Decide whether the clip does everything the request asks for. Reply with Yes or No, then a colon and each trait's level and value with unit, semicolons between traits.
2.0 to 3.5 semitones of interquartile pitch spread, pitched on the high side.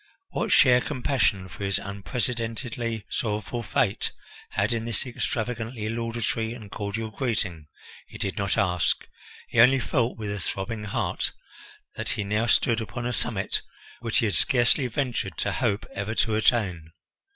No: average, 2.9 semitones; low, 115 Hz